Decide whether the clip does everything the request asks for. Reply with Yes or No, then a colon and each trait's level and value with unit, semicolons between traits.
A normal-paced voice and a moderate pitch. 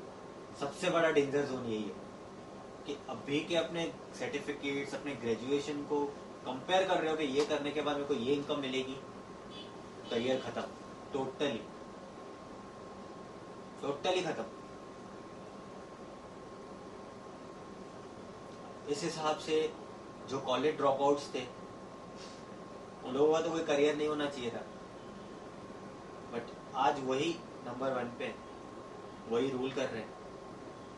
Yes: average, 120 wpm; medium, 145 Hz